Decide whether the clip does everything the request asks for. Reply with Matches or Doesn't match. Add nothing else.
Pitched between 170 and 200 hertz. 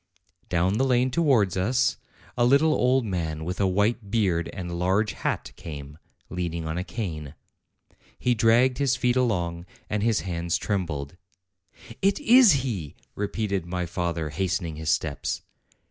Doesn't match